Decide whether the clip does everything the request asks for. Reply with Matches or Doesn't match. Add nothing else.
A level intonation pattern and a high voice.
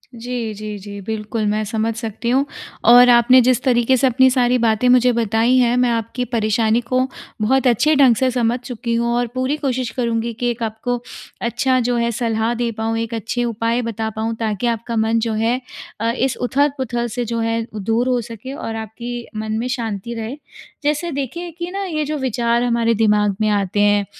Matches